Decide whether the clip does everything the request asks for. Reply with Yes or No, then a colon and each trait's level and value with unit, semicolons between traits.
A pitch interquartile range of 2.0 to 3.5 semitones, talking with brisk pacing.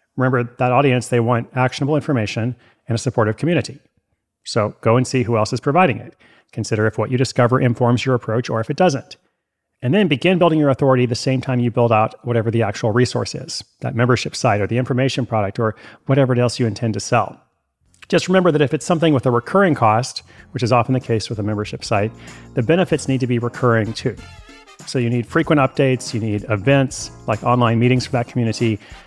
Yes: average, 2.8 semitones; fast, 215 wpm